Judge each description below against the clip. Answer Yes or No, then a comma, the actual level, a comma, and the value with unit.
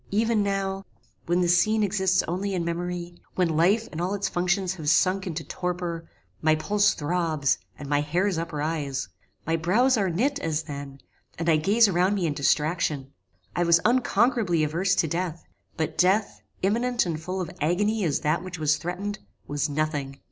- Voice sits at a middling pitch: Yes, medium, 175 Hz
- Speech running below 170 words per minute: No, average, 175 wpm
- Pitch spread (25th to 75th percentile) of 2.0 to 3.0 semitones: No, average, 3.8 semitones